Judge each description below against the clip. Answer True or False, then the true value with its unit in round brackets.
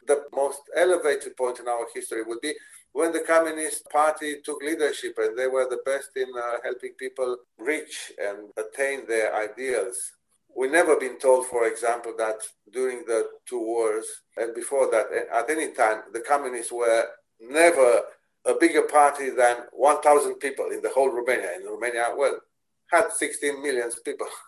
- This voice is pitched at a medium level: True (165 Hz)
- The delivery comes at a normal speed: True (165 wpm)